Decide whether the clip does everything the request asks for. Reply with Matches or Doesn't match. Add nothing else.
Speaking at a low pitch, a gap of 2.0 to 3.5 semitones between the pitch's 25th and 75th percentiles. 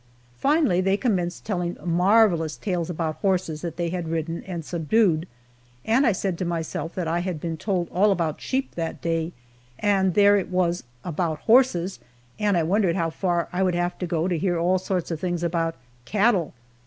Doesn't match